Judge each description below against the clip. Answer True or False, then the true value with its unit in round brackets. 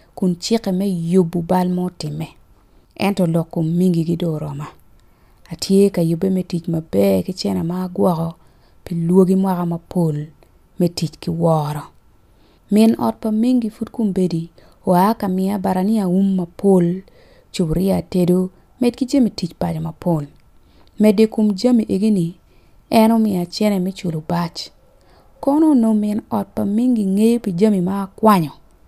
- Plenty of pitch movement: False (3.9 semitones)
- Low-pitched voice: False (185 Hz)